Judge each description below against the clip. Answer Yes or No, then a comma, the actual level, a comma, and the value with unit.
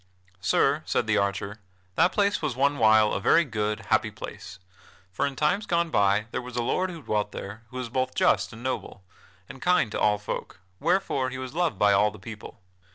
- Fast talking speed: Yes, fast, 210 wpm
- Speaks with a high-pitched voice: No, low, 120 Hz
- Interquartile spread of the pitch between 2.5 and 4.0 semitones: No, wide, 5.6 semitones